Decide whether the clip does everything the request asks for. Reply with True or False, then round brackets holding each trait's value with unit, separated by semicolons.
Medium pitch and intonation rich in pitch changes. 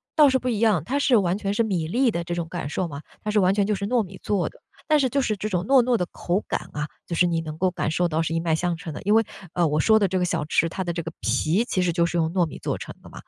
False (180 Hz; 4.4 semitones)